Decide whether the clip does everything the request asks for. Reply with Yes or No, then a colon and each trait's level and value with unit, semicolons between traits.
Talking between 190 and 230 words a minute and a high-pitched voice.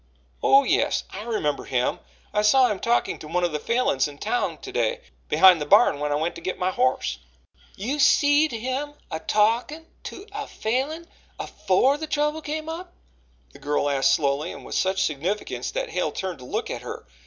Yes: average, 195 wpm; high, 220 Hz